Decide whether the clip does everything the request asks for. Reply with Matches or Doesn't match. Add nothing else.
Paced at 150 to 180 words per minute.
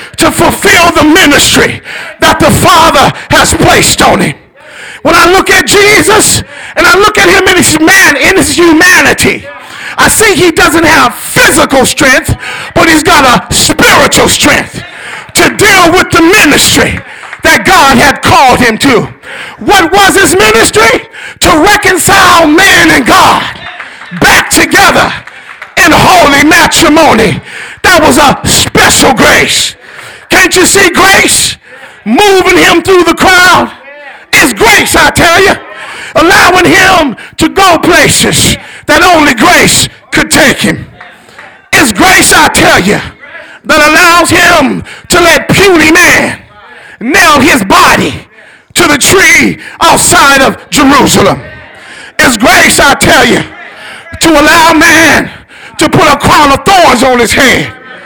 Doesn't match